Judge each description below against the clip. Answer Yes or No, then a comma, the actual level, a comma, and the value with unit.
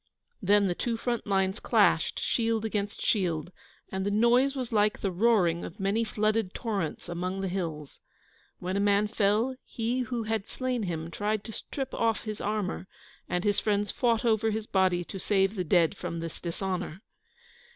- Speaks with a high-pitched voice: Yes, high, 205 Hz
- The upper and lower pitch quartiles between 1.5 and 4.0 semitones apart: Yes, average, 3.3 semitones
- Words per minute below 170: No, average, 175 wpm